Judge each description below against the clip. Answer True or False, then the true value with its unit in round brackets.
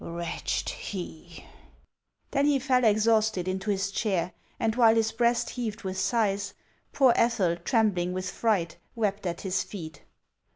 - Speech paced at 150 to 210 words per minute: False (140 wpm)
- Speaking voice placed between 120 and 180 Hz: False (205 Hz)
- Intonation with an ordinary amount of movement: True (3.7 semitones)